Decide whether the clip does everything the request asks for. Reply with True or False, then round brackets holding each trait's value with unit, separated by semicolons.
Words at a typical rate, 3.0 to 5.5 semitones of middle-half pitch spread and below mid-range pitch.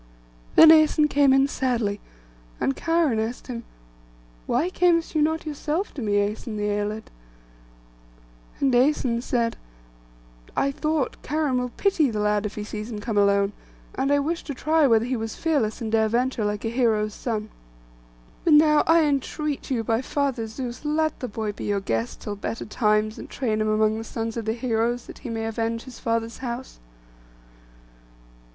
False (175 wpm; 4.7 semitones; 235 Hz)